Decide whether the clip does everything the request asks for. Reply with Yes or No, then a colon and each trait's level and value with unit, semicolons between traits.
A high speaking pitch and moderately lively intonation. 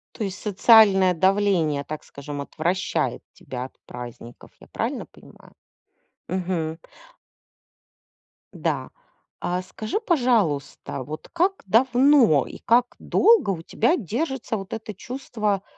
No: high, 195 Hz; wide, 7.1 semitones